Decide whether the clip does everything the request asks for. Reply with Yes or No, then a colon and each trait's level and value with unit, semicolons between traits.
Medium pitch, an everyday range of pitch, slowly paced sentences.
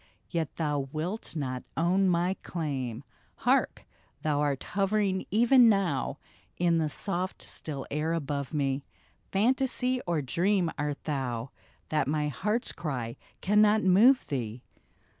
No: medium, 165 Hz; wide, 5.7 semitones; slow, 125 wpm